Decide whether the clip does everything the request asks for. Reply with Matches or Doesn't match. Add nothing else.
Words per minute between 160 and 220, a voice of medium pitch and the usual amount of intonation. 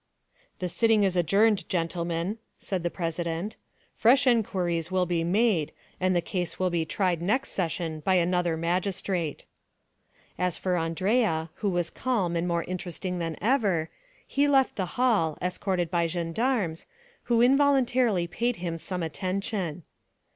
Doesn't match